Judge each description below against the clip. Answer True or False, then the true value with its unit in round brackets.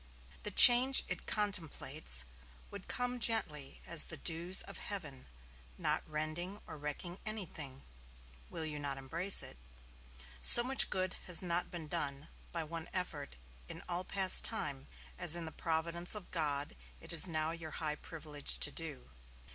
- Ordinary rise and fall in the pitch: True (3.7 semitones)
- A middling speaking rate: True (155 wpm)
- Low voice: False (165 Hz)